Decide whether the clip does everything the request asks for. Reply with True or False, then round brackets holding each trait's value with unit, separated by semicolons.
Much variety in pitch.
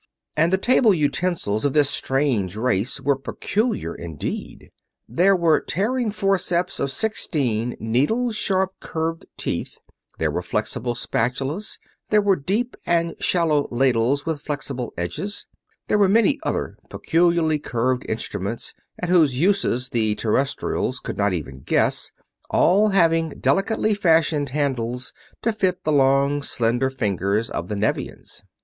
True (7.1 semitones)